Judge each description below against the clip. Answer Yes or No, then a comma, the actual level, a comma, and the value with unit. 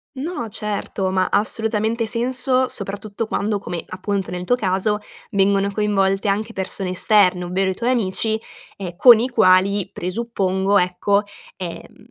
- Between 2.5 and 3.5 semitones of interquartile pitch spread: Yes, average, 2.8 semitones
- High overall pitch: Yes, high, 200 Hz